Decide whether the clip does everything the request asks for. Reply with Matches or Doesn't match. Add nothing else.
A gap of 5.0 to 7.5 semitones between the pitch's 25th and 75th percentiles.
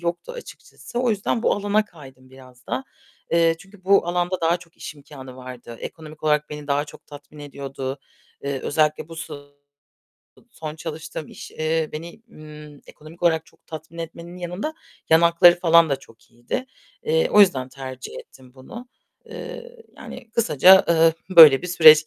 Doesn't match